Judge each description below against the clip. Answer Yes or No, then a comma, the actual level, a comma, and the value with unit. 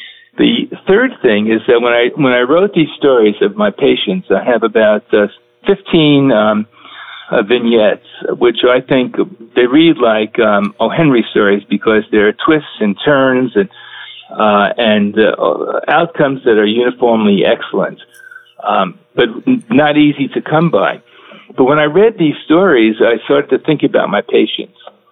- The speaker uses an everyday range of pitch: No, wide, 6.7 semitones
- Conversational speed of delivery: Yes, average, 160 wpm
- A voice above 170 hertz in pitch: No, low, 125 Hz